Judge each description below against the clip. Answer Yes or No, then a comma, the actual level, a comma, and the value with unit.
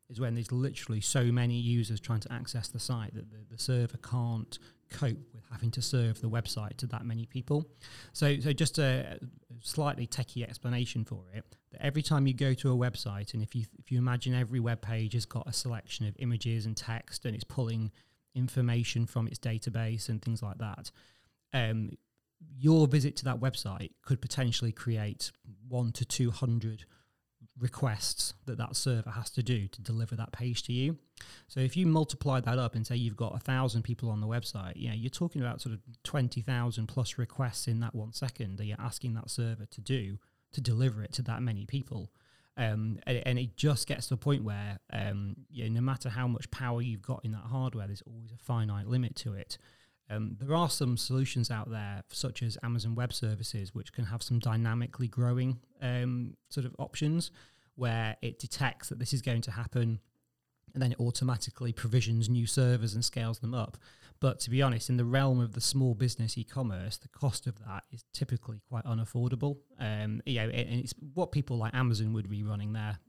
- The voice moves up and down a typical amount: No, narrow, 2.3 semitones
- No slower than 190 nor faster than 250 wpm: Yes, fast, 205 wpm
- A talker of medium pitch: No, low, 120 Hz